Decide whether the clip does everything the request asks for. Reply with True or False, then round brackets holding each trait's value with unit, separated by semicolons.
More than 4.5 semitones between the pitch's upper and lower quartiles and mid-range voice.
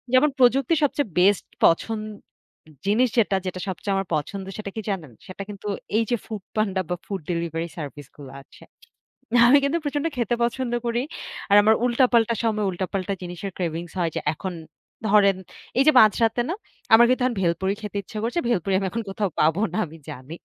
False (4.9 semitones; 200 Hz)